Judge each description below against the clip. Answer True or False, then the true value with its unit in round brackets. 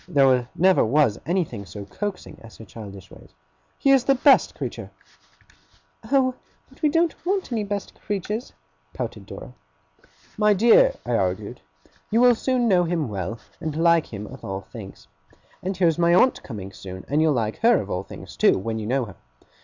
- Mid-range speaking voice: True (165 Hz)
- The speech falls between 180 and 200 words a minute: True (185 wpm)